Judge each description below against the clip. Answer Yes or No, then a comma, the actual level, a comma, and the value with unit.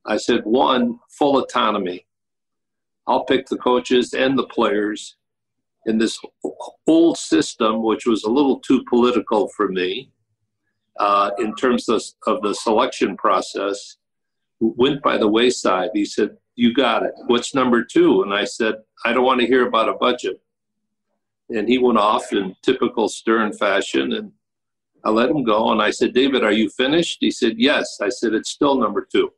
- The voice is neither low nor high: No, low, 125 Hz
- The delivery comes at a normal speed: Yes, average, 170 wpm